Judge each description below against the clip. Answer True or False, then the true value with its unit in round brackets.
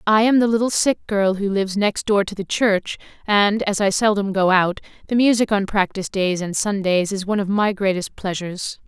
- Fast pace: True (215 wpm)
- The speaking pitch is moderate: False (200 Hz)